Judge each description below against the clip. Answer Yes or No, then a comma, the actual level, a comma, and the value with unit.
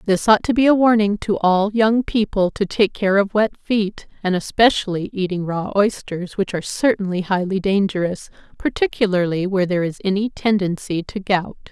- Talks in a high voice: Yes, high, 200 Hz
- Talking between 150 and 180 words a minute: Yes, average, 175 wpm